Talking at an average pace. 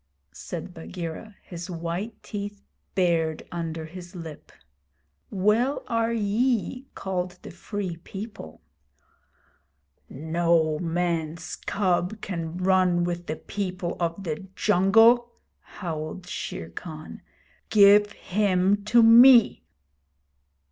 No: slow, 100 wpm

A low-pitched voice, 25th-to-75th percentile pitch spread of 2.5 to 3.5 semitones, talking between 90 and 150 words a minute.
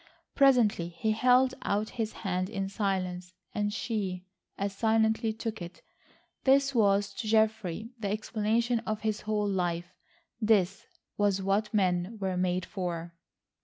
No: high, 205 Hz; average, 3.1 semitones; slow, 135 wpm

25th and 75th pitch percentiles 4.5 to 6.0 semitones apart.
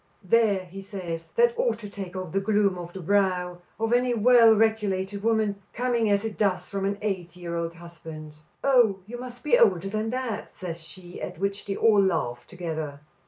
No: average, 3.9 semitones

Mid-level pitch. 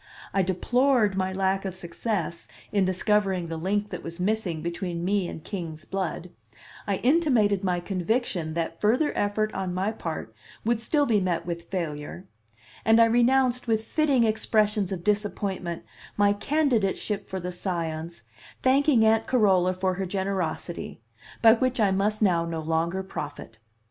No: high, 195 Hz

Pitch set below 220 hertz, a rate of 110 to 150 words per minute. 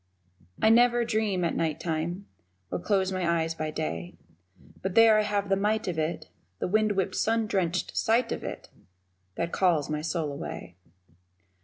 No: medium, 185 Hz; average, 170 wpm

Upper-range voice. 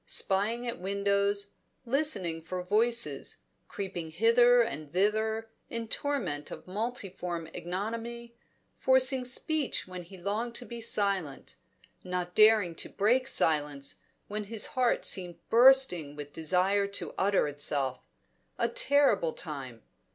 Yes: high, 200 Hz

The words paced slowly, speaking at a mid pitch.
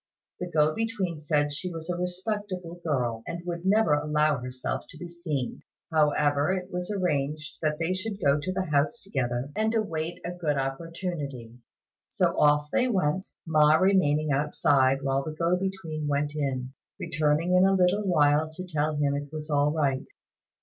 No: average, 170 wpm; medium, 155 Hz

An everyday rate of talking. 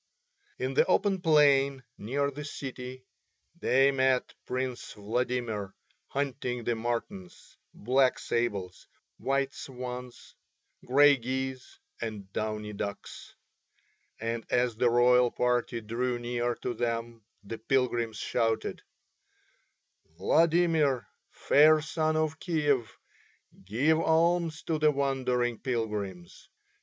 No: slow, 105 wpm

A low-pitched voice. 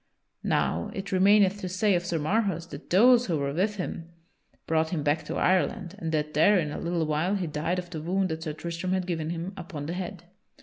No: medium, 175 Hz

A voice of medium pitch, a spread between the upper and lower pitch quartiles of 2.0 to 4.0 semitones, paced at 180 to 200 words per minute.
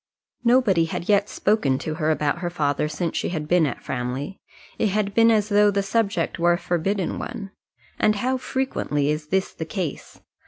No: medium, 180 Hz; average, 5.1 semitones; average, 190 wpm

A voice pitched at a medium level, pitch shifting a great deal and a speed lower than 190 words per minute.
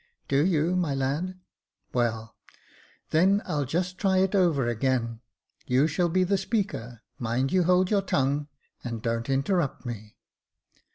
Yes: medium, 150 Hz; wide, 6.9 semitones; average, 155 wpm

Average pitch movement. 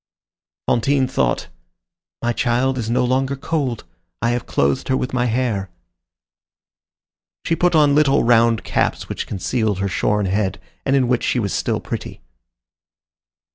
Yes: average, 3.6 semitones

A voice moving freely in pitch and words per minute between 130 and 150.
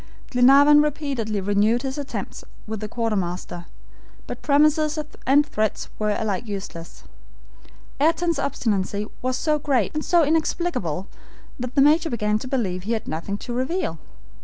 Yes: wide, 6.2 semitones; average, 140 wpm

